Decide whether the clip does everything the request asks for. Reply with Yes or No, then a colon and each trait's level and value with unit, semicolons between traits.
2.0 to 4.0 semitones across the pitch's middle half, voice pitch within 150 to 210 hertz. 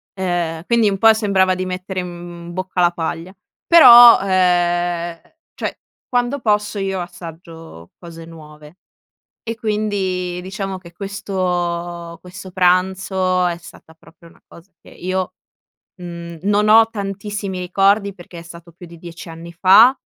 Yes: narrow, 2.6 semitones; medium, 185 Hz